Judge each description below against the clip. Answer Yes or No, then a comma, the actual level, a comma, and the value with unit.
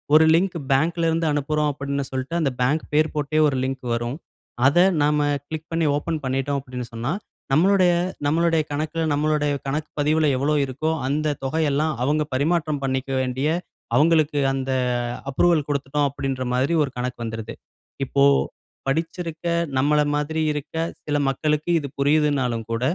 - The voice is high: No, medium, 145 Hz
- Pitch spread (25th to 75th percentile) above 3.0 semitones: No, average, 2.7 semitones